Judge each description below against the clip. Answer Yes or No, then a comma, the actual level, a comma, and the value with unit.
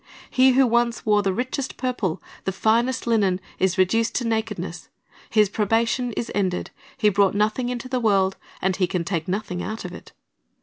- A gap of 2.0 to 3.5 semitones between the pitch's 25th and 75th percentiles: No, average, 3.9 semitones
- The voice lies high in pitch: Yes, high, 215 Hz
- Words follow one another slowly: No, average, 180 wpm